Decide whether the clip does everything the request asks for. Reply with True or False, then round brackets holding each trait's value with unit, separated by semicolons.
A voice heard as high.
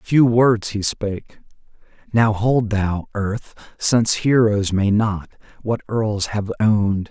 False (105 Hz)